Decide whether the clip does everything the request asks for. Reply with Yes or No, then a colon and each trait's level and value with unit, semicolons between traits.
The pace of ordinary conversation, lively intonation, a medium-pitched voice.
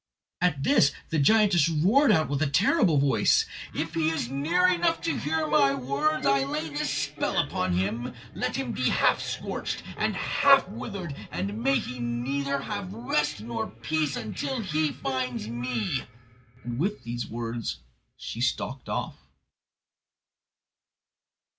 No: average, 145 wpm; average, 4.9 semitones; medium, 145 Hz